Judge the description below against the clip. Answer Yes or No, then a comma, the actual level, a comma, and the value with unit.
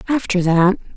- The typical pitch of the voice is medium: No, high, 195 Hz